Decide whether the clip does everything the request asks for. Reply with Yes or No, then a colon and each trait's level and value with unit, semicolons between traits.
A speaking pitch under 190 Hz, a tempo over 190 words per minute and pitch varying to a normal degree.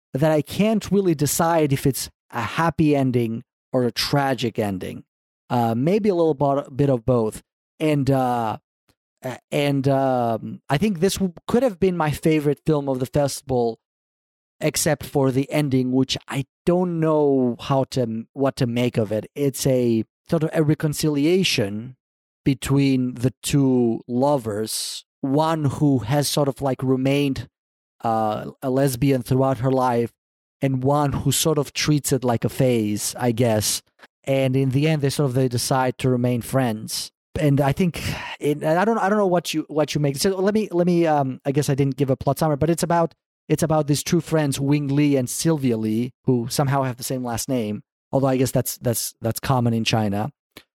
No: low, 135 Hz; average, 185 wpm; average, 3.4 semitones